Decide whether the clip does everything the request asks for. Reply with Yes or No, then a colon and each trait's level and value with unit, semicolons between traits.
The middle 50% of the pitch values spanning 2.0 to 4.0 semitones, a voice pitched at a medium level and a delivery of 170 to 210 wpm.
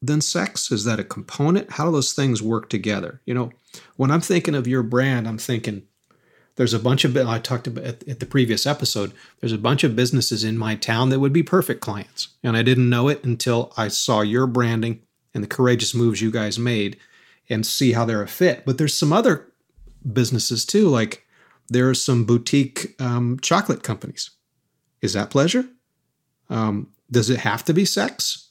No: average, 3.6 semitones; low, 125 Hz; average, 200 wpm